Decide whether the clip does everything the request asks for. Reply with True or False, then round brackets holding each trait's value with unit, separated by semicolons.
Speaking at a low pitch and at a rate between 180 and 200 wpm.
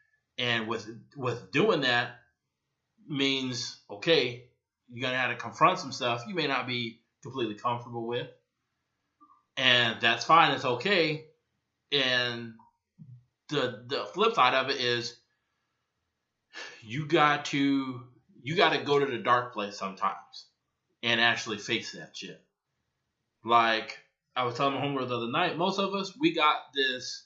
False (125 Hz; 145 wpm)